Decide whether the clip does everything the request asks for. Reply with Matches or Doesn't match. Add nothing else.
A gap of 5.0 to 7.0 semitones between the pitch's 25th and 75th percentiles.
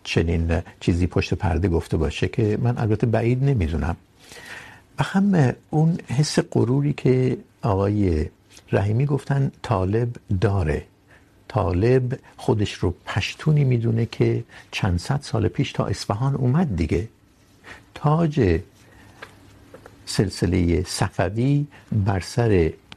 Matches